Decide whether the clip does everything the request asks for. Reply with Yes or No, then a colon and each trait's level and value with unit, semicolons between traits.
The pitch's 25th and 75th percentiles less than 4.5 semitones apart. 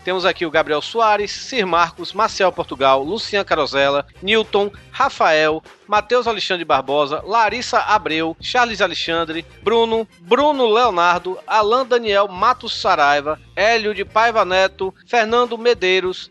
No: average, 5.2 semitones